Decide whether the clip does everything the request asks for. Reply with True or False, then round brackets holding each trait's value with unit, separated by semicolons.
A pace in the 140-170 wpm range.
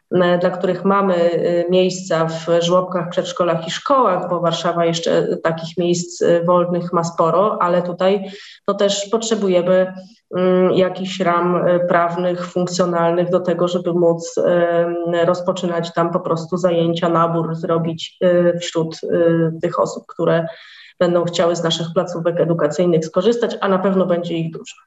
False (130 wpm)